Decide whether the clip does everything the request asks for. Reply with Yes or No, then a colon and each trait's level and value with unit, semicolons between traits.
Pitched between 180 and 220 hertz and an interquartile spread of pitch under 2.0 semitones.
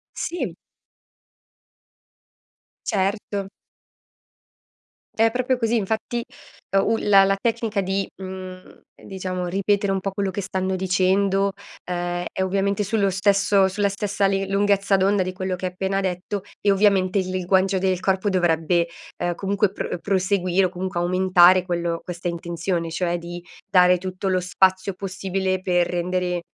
Yes: high, 190 Hz; narrow, 1.5 semitones